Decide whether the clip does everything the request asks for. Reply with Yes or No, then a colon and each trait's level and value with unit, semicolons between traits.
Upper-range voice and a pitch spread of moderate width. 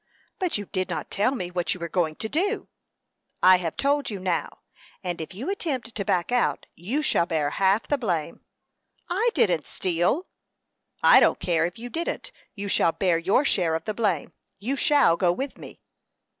No: high, 195 Hz; wide, 7.2 semitones